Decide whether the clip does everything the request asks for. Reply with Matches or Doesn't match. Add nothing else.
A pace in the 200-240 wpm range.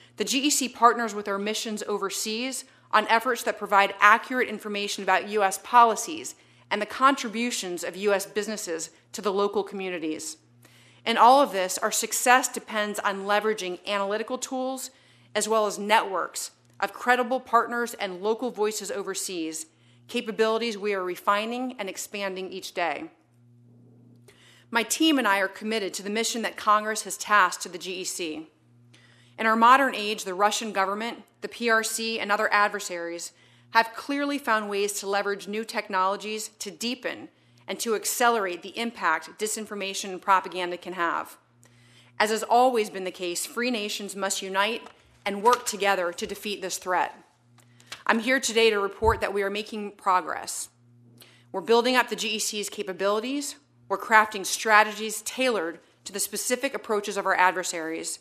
Doesn't match